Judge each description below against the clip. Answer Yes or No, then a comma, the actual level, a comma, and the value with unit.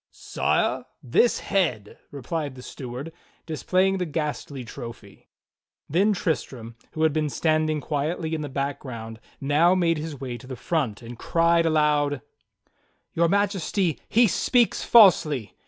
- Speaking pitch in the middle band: Yes, medium, 155 Hz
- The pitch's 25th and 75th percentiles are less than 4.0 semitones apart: No, average, 4.3 semitones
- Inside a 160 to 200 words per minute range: No, average, 140 wpm